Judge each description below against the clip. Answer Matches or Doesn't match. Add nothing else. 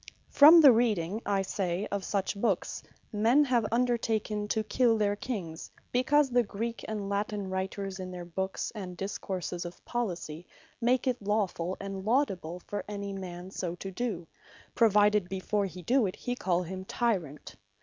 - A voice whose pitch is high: Matches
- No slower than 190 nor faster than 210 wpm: Doesn't match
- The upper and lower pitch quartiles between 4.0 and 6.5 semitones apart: Doesn't match